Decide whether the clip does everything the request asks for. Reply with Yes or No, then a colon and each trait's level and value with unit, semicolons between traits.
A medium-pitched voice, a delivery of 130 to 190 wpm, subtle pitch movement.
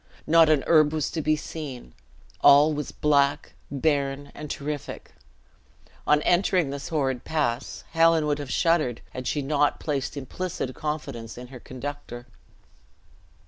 Yes: medium, 145 Hz; average, 140 wpm; narrow, 2.3 semitones